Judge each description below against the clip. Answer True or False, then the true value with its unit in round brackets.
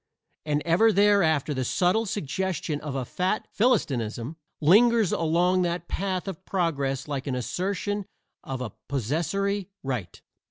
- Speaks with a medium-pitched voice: True (170 Hz)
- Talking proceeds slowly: True (130 wpm)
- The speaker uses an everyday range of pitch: False (6.2 semitones)